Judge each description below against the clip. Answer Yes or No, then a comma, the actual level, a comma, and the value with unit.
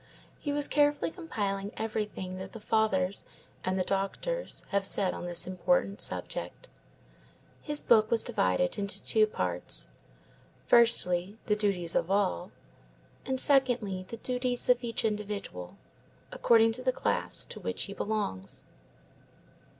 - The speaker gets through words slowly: Yes, slow, 130 wpm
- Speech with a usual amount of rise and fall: Yes, average, 4.2 semitones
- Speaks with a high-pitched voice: Yes, high, 210 Hz